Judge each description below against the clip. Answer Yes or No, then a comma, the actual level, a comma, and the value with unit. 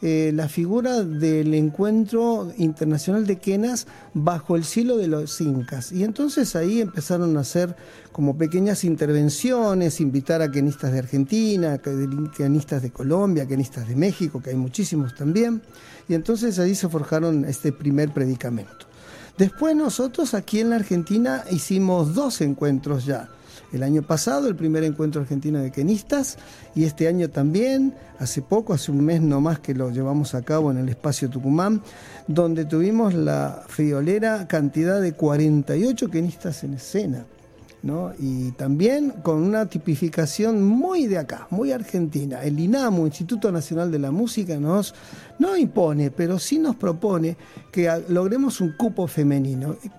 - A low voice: No, medium, 165 Hz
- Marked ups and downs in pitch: Yes, wide, 5.8 semitones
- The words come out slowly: No, average, 150 wpm